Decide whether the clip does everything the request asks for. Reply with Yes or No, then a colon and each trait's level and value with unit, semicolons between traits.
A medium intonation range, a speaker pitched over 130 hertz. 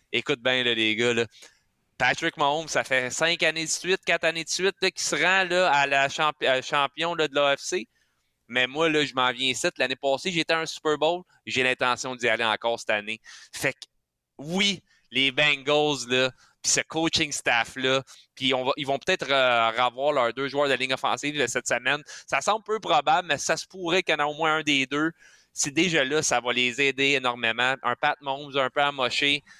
Yes: average, 4.0 semitones; medium, 140 Hz